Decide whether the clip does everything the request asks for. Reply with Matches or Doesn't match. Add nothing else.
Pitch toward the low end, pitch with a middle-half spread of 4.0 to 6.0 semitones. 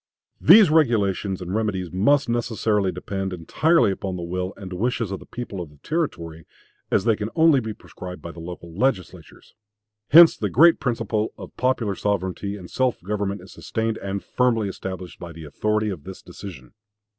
Matches